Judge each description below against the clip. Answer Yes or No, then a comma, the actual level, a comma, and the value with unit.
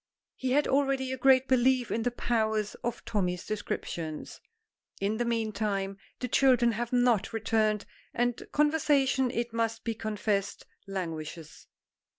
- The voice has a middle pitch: No, high, 230 Hz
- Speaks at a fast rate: No, slow, 135 wpm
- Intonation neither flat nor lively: Yes, average, 3.6 semitones